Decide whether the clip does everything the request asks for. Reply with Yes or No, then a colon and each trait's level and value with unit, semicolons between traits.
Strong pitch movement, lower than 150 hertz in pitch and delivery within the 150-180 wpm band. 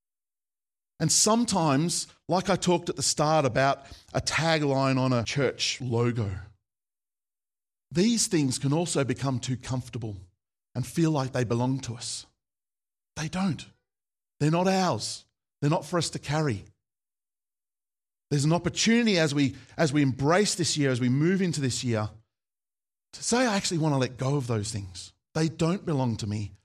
Yes: wide, 5.7 semitones; medium, 140 Hz; average, 160 wpm